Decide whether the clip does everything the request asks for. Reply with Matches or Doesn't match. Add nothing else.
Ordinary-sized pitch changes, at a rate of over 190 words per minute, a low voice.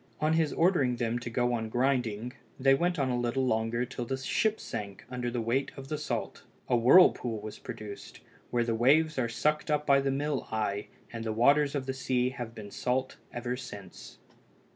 Matches